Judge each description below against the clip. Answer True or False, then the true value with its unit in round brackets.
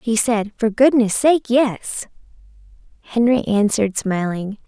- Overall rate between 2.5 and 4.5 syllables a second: True (4.1 syllables/s)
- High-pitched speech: True (225 Hz)